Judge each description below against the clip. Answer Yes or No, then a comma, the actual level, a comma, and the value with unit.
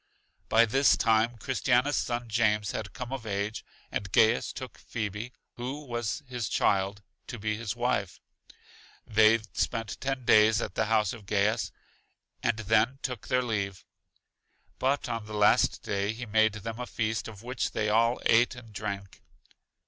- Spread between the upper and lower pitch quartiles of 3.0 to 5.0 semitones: No, narrow, 2.5 semitones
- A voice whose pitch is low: Yes, low, 110 Hz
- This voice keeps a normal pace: Yes, average, 160 wpm